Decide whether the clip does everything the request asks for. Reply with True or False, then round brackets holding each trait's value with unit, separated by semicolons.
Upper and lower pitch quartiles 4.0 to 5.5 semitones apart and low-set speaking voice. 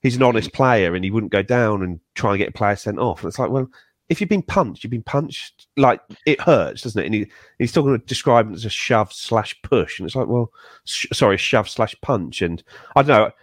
True (4.3 semitones; 115 Hz)